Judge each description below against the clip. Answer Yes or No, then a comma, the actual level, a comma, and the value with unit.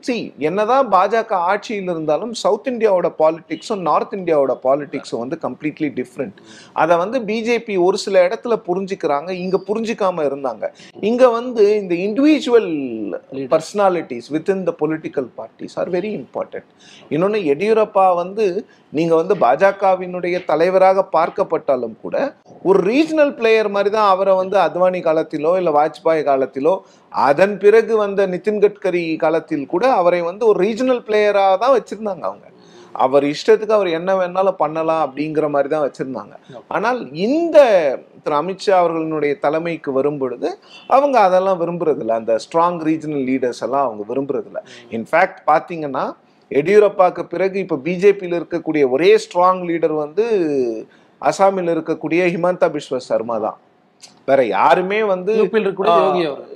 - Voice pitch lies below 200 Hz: Yes, medium, 185 Hz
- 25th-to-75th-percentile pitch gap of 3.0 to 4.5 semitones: No, average, 4.9 semitones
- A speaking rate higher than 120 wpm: Yes, fast, 130 wpm